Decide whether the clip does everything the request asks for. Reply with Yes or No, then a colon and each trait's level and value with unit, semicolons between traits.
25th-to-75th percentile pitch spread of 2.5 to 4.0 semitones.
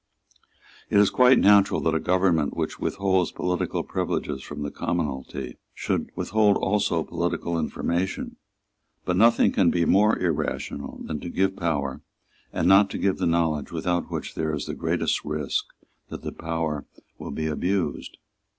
Yes: average, 3.7 semitones